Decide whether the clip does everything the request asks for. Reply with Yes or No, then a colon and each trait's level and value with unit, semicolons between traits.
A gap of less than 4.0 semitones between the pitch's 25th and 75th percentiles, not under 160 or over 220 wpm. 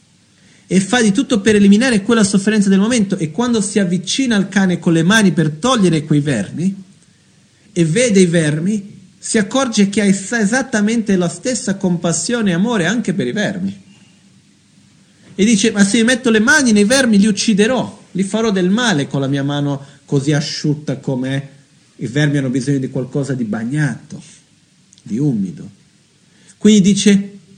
No: average, 4.7 semitones; fast, 170 wpm